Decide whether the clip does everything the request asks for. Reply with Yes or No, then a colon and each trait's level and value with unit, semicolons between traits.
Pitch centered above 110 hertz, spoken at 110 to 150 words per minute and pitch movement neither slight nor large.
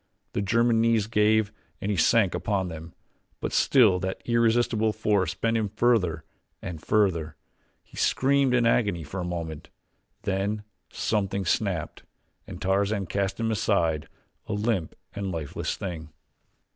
No: low, 100 Hz; average, 140 wpm; average, 3.9 semitones